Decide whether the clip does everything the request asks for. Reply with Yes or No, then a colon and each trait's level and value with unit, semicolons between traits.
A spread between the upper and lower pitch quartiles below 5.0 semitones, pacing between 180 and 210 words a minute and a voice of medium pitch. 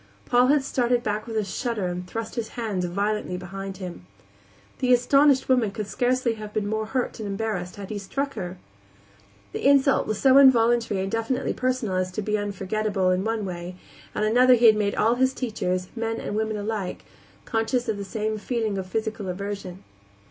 No: average, 3.6 semitones; average, 190 wpm; high, 215 Hz